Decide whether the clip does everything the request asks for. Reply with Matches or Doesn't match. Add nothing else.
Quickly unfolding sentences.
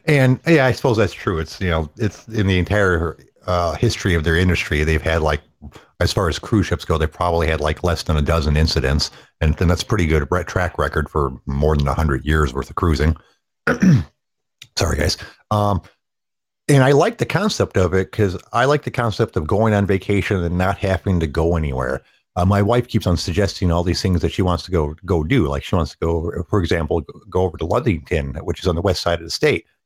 Matches